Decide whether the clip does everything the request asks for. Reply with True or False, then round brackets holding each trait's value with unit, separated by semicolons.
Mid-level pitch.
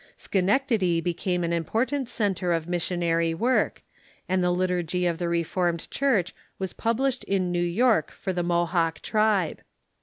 True (180 Hz)